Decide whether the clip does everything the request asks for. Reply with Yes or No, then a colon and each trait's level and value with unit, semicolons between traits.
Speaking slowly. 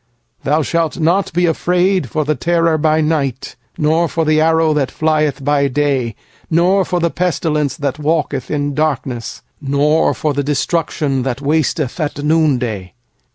No: average, 145 wpm